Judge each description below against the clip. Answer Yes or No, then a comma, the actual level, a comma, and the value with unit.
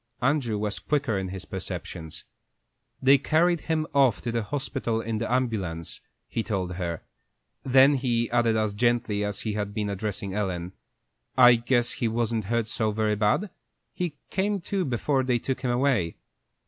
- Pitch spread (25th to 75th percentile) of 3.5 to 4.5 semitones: Yes, average, 4.2 semitones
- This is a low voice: Yes, low, 115 Hz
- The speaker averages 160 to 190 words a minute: Yes, average, 170 wpm